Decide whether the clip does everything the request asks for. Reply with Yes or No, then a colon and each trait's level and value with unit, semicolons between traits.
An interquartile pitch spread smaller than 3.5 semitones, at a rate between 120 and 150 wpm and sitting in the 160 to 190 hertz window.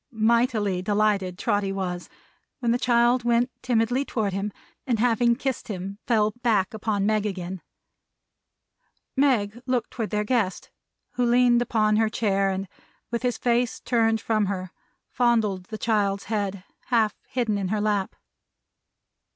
No: average, 3.1 semitones; average, 145 wpm; high, 215 Hz